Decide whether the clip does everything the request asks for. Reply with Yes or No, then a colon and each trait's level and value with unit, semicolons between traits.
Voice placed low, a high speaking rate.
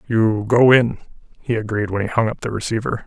Yes: low, 110 Hz; fast, 215 wpm